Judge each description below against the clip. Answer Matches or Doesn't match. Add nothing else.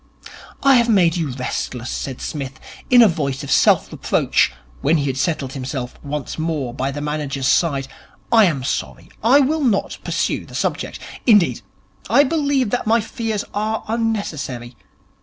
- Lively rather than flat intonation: Matches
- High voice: Doesn't match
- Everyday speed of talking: Matches